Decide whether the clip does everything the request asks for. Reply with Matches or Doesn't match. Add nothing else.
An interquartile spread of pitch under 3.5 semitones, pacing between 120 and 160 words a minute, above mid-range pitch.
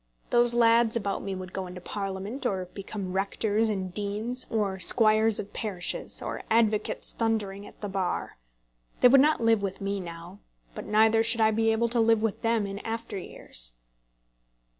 Doesn't match